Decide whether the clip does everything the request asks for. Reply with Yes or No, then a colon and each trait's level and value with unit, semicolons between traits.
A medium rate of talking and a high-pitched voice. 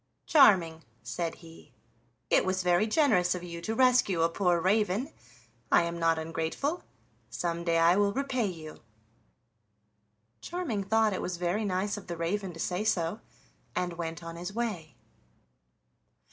No: average, 150 wpm; medium, 180 Hz